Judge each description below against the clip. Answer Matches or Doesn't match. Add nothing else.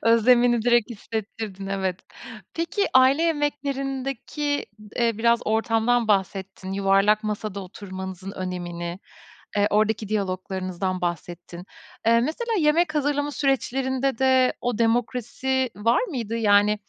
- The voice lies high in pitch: Matches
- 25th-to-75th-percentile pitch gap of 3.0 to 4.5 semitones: Doesn't match